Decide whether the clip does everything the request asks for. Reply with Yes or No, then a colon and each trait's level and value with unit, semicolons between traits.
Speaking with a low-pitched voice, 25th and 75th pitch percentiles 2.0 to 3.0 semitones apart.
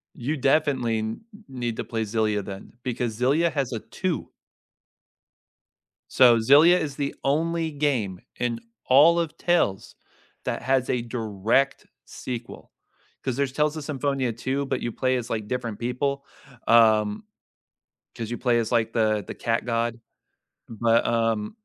No: low, 125 Hz; average, 3.5 semitones